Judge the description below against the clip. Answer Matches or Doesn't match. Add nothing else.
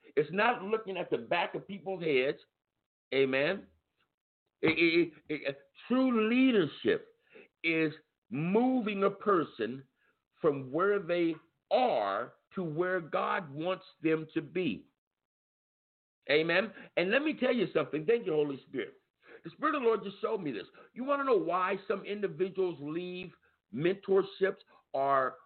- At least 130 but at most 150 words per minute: Matches